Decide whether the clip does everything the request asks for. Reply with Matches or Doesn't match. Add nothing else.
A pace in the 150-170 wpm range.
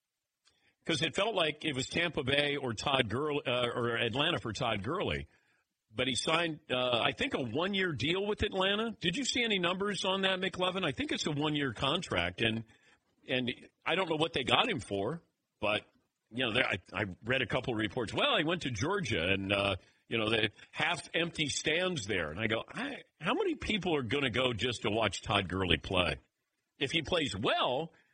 Doesn't match